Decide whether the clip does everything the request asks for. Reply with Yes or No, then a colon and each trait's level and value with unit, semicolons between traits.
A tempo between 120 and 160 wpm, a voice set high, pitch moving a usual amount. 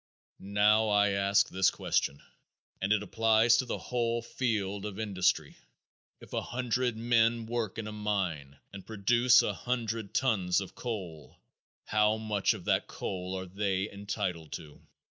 No: average, 150 wpm; low, 105 Hz; average, 3.0 semitones